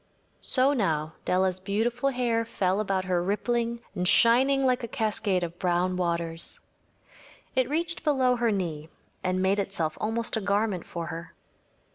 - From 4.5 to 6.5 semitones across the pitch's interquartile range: Yes, average, 4.8 semitones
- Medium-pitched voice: No, high, 200 Hz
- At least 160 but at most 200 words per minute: No, average, 150 wpm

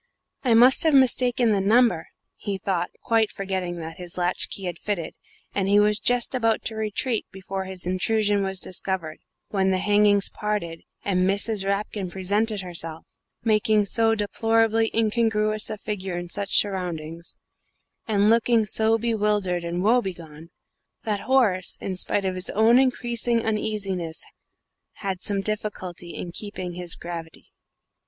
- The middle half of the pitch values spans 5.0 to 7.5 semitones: No, average, 3.3 semitones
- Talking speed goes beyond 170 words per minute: No, average, 145 wpm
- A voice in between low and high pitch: No, high, 205 Hz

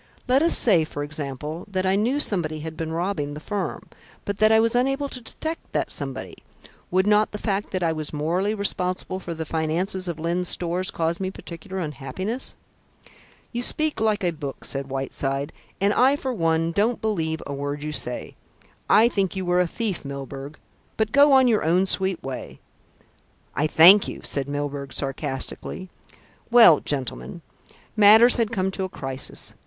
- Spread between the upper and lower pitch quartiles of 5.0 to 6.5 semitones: Yes, wide, 5.6 semitones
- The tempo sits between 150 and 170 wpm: No, average, 180 wpm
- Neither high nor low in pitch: Yes, medium, 180 Hz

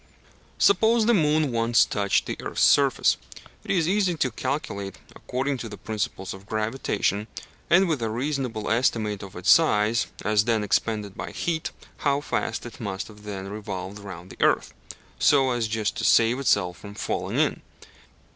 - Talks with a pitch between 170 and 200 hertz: No, low, 110 Hz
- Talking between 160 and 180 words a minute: Yes, average, 165 wpm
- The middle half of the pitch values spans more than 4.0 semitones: Yes, average, 5.2 semitones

